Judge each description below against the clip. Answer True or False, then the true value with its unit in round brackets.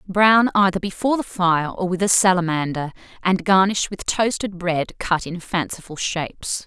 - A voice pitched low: False (185 Hz)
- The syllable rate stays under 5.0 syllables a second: True (4.7 syllables/s)